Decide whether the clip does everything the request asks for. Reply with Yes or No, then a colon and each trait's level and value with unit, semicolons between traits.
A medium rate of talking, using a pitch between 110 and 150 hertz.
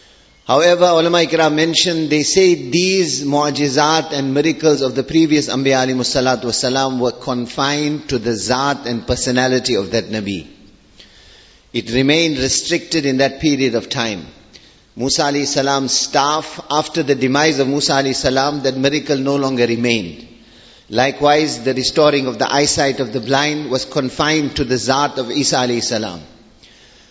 Yes: average, 145 wpm; low, 135 Hz